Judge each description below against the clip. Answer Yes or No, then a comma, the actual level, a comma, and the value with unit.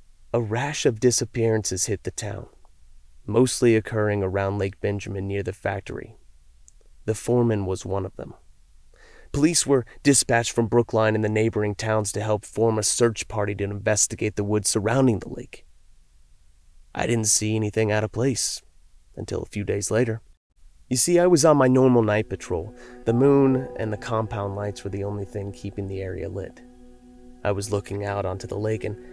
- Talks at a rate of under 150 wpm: No, average, 175 wpm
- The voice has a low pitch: Yes, low, 110 Hz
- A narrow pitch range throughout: No, average, 3.2 semitones